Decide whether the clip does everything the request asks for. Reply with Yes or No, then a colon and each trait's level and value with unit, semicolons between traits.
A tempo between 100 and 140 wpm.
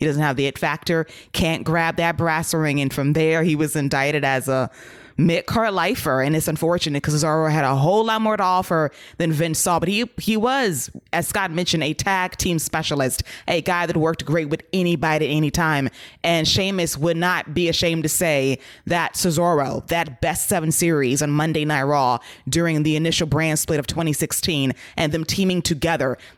No: average, 195 wpm